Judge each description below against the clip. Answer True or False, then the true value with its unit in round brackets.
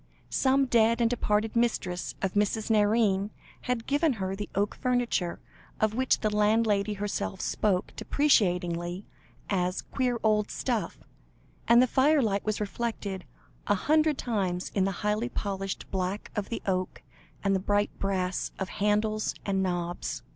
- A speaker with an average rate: True (145 wpm)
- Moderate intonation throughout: True (3.3 semitones)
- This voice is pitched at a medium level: False (210 Hz)